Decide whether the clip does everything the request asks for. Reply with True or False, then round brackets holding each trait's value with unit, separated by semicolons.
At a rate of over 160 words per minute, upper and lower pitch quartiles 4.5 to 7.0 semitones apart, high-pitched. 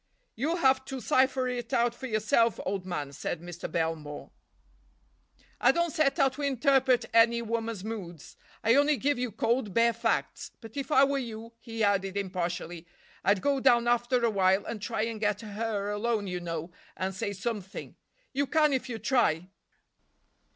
True (170 wpm; 4.8 semitones; 230 Hz)